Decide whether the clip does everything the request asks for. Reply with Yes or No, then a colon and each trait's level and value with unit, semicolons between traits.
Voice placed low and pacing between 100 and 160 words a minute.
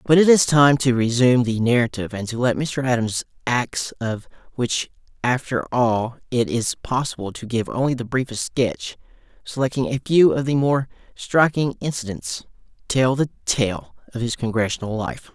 Yes: low, 125 Hz; average, 155 wpm